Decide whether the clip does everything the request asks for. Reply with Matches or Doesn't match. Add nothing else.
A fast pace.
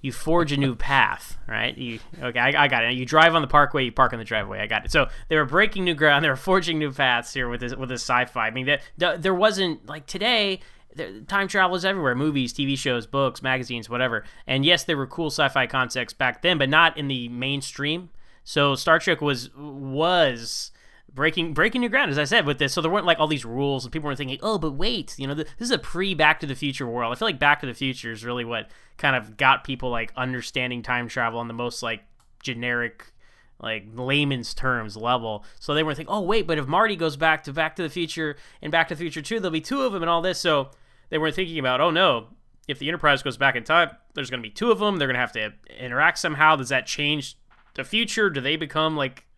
Matches